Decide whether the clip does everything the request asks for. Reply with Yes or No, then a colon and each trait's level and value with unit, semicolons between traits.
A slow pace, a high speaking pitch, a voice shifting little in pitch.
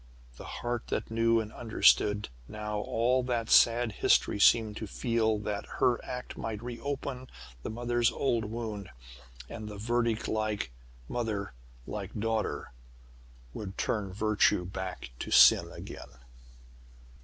No: slow, 130 wpm; low, 110 Hz; narrow, 2.2 semitones